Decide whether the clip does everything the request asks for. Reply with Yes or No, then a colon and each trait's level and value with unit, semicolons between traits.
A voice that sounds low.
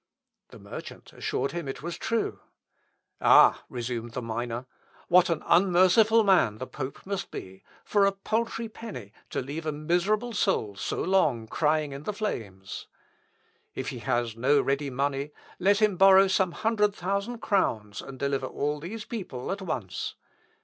No: medium, 160 Hz